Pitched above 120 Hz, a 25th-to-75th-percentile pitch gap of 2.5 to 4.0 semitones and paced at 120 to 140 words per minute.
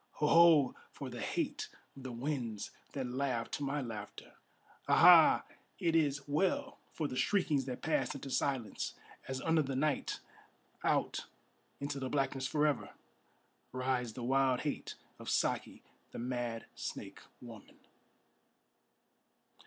Yes: low, 135 Hz; average, 2.9 semitones; slow, 135 wpm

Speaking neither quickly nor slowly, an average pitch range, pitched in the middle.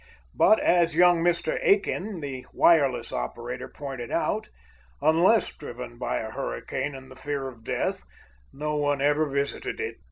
Yes: average, 150 wpm; average, 4.5 semitones; medium, 145 Hz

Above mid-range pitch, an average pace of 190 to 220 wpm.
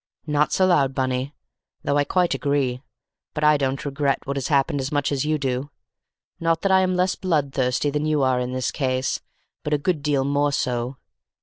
No: medium, 145 Hz; average, 200 wpm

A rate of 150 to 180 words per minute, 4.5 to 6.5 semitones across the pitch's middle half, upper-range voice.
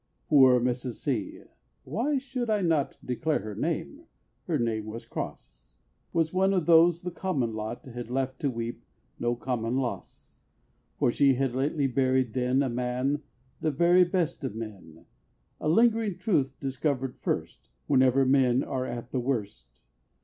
No: average, 155 wpm; average, 4.8 semitones; low, 130 Hz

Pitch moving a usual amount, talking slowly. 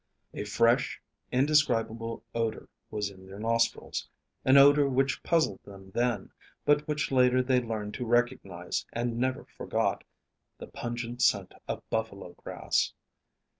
Yes: average, 3.1 semitones; slow, 130 wpm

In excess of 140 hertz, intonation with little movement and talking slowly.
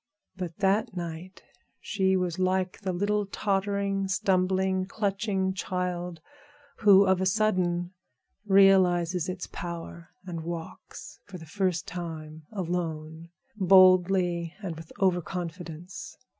Yes: medium, 185 Hz; narrow, 1.9 semitones; slow, 115 wpm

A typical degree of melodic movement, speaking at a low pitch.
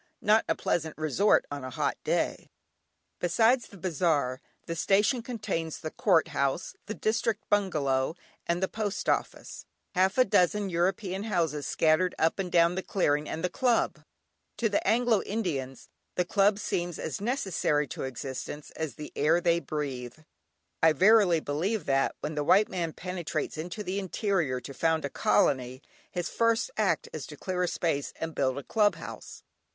No: average, 5.0 semitones; medium, 175 Hz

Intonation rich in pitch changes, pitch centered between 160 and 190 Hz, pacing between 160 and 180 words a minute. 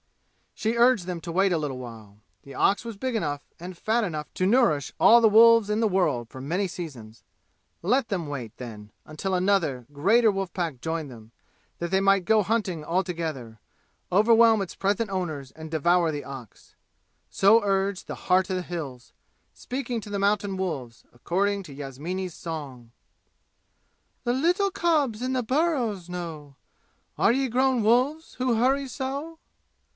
Yes: wide, 7.0 semitones; medium, 185 Hz; average, 165 wpm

